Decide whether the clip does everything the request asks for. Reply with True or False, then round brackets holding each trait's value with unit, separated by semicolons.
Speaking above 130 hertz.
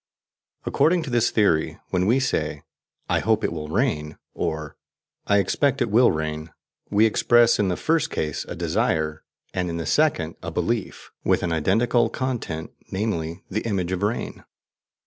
False (100 Hz)